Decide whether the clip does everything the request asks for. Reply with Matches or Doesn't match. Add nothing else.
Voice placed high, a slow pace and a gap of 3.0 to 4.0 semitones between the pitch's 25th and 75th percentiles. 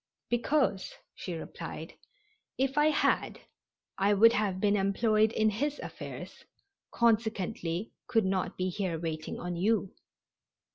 Matches